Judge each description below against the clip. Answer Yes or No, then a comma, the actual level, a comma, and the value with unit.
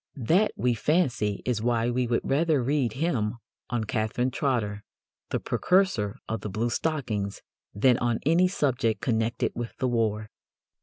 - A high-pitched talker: No, low, 120 Hz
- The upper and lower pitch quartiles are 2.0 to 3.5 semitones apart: No, average, 4.1 semitones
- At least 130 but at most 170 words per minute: Yes, average, 145 wpm